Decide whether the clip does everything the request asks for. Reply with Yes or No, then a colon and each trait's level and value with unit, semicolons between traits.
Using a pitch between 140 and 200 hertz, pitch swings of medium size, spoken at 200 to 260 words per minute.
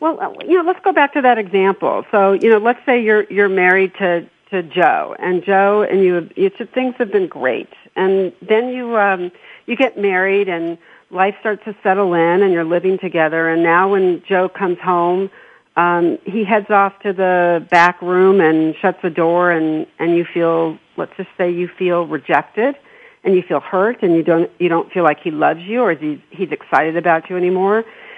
Yes: high, 190 Hz; average, 3.6 semitones; fast, 205 wpm